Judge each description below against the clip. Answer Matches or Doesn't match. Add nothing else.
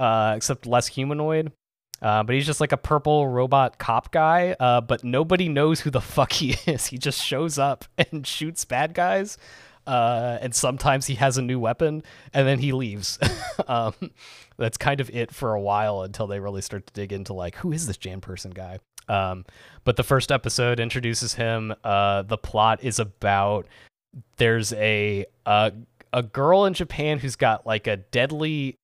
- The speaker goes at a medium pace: Matches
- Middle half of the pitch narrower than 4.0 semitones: Doesn't match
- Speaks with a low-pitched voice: Matches